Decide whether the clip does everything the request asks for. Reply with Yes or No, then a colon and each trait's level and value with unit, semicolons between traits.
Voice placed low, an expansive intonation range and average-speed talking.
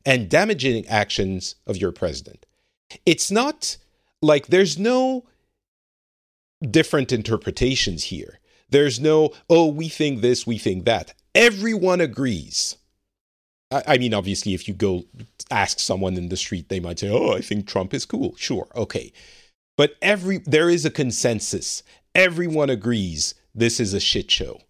Yes: low, 125 Hz; wide, 8.1 semitones; average, 150 wpm